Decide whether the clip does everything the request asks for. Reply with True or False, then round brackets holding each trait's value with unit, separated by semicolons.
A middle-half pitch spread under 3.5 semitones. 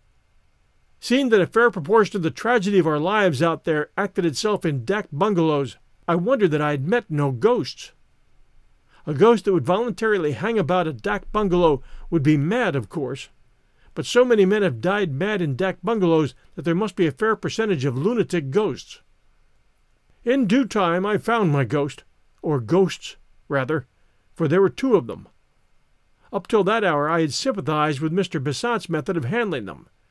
False (5.3 semitones)